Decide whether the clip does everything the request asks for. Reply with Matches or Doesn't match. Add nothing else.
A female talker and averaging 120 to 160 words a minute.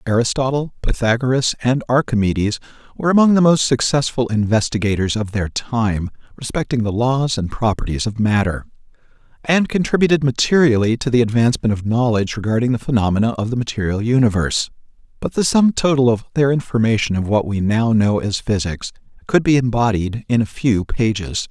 Doesn't match